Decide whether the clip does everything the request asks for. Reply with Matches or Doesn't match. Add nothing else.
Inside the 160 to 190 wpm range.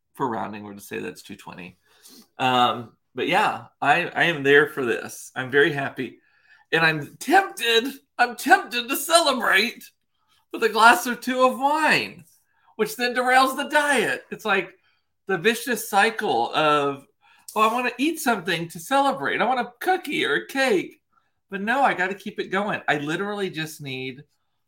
Matches